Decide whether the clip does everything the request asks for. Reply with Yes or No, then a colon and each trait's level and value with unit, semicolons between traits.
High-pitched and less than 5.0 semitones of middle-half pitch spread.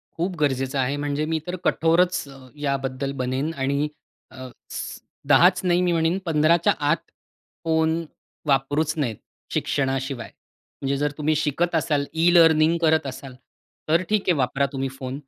No: medium, 150 Hz; average, 3.3 semitones